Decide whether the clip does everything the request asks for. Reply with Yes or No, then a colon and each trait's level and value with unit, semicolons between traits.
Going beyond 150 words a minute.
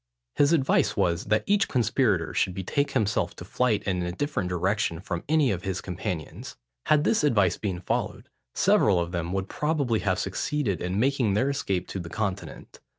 Yes: average, 180 wpm